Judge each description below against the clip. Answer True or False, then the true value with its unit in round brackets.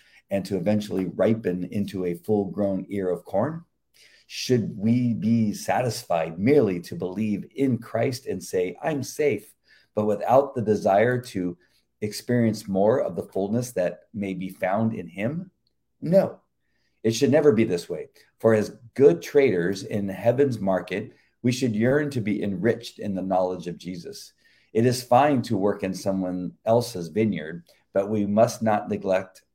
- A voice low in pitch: True (105 Hz)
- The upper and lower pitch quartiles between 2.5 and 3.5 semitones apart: False (4.1 semitones)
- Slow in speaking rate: False (160 wpm)